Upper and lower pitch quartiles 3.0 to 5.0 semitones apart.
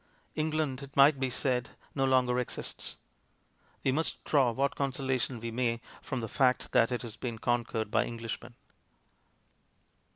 No: narrow, 2.4 semitones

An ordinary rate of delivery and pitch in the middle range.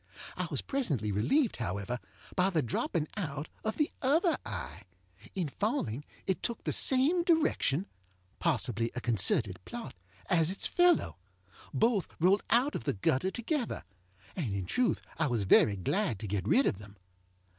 Yes: average, 155 wpm; medium, 165 Hz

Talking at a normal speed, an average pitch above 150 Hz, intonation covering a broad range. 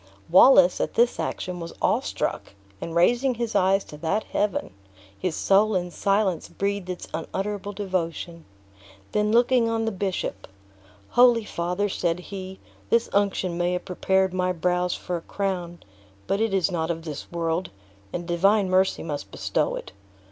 No: average, 160 wpm; medium, 185 Hz; average, 2.9 semitones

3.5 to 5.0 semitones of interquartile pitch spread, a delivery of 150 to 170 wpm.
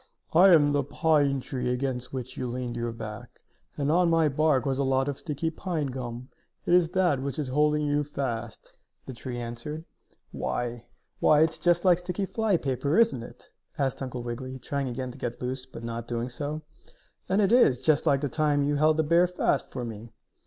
No: average, 4.0 semitones; average, 200 wpm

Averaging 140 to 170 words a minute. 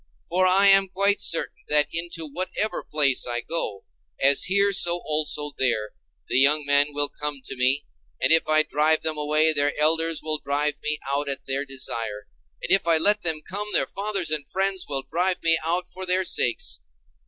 No: average, 190 wpm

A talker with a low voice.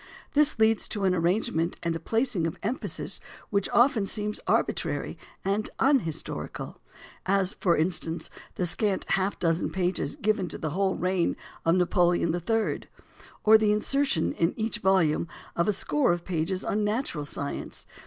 No: high, 190 Hz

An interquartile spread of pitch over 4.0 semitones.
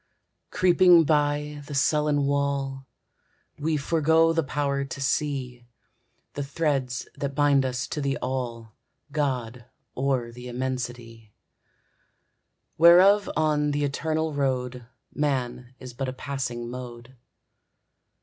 No: average, 2.9 semitones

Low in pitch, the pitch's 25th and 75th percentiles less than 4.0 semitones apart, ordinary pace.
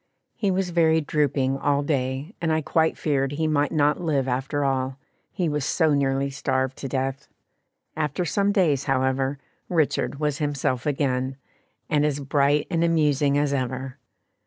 No: medium, 145 Hz; narrow, 2.6 semitones; average, 160 wpm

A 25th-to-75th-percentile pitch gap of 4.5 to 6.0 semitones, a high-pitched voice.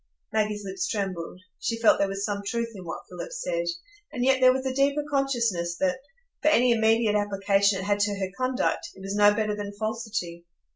No: average, 3.8 semitones; high, 210 Hz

